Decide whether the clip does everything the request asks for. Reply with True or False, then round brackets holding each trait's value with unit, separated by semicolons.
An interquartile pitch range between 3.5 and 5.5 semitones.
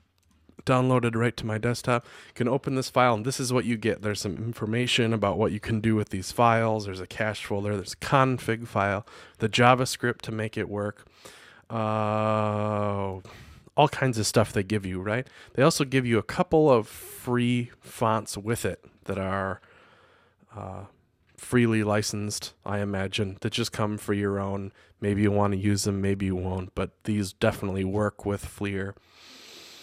False (3.0 semitones)